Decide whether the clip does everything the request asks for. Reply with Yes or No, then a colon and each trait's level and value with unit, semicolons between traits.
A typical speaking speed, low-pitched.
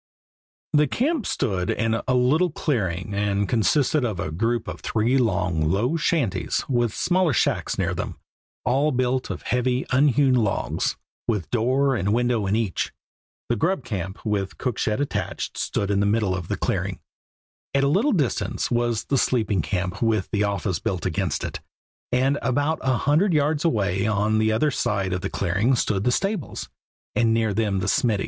Yes: average, 175 wpm; low, 115 Hz